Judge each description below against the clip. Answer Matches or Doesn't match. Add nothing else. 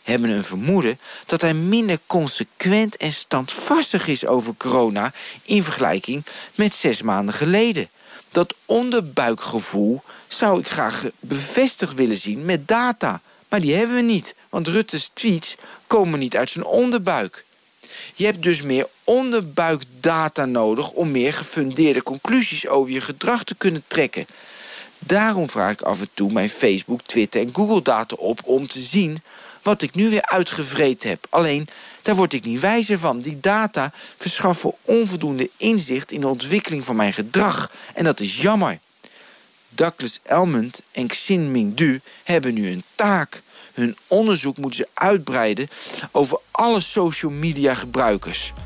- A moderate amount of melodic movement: Doesn't match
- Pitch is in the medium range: Matches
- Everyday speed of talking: Matches